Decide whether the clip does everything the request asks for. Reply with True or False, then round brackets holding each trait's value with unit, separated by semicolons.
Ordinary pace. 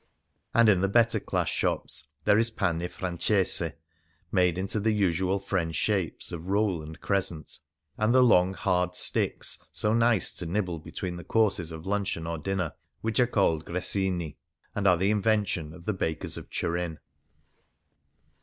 True (160 wpm)